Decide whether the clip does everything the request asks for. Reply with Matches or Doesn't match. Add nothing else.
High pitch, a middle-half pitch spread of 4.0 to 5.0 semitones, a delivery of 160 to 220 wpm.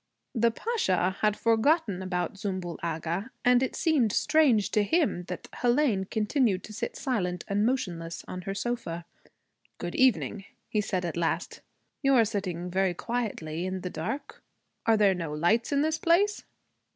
Doesn't match